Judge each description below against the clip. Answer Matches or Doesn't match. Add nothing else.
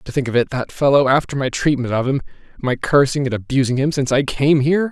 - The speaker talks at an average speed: Doesn't match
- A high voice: Doesn't match